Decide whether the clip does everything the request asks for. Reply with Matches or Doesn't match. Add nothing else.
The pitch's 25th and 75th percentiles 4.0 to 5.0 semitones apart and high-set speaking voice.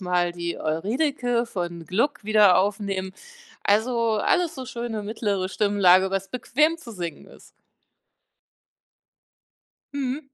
Matches